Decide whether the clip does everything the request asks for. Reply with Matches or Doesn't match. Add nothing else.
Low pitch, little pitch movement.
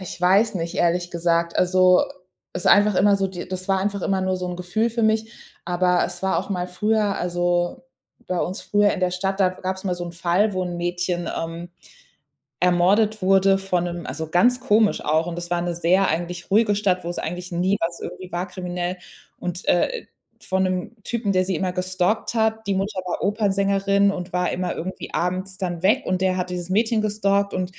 Doesn't match